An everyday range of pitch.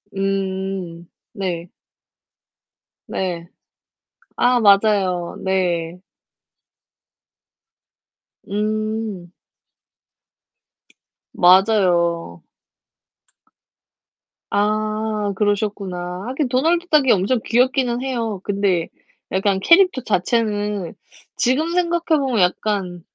Yes: average, 4.5 semitones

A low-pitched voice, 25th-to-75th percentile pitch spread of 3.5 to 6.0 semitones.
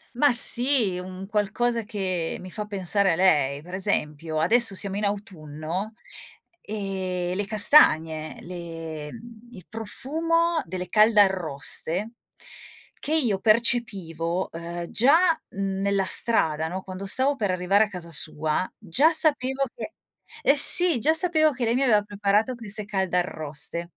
No: high, 200 Hz; average, 5.2 semitones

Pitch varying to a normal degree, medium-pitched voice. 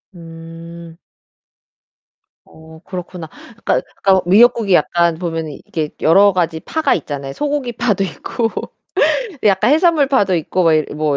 Yes: average, 5.0 semitones; medium, 175 Hz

